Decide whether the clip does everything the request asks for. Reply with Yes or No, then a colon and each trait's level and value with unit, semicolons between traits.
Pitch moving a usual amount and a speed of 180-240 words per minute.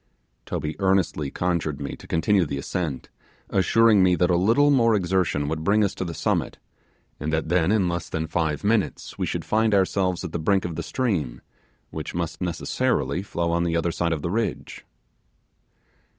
Yes: average, 3.6 semitones; average, 185 wpm